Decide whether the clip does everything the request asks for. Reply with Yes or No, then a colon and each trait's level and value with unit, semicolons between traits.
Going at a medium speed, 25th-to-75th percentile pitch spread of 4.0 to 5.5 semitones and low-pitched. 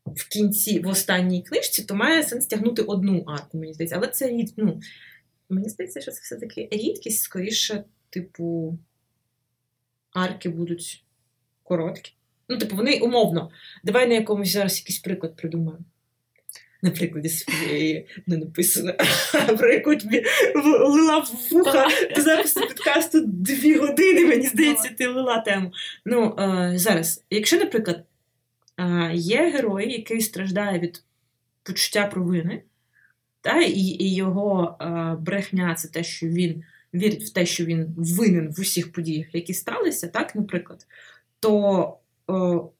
No: average, 130 wpm; average, 4.8 semitones; medium, 185 Hz